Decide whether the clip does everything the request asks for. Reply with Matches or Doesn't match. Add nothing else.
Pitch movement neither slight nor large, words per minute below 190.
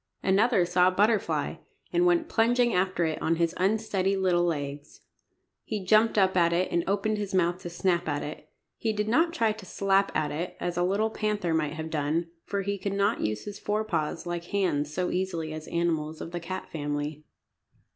Doesn't match